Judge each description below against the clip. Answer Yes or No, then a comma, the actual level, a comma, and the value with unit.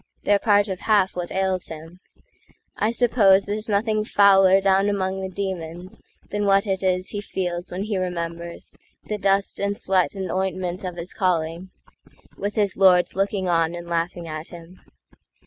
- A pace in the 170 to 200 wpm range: No, average, 150 wpm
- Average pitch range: No, narrow, 2.2 semitones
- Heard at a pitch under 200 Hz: Yes, high, 190 Hz